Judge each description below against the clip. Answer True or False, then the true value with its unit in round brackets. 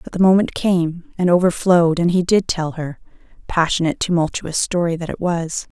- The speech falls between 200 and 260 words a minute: False (165 wpm)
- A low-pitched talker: False (170 Hz)